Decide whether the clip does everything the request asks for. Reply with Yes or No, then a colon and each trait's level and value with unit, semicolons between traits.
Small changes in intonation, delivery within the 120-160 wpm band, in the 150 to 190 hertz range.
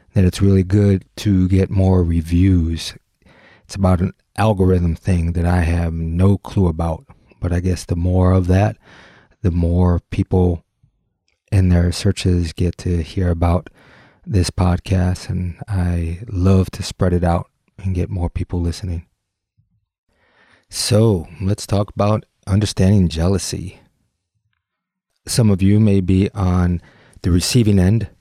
No: narrow, 2.3 semitones; average, 140 wpm; very low, 95 Hz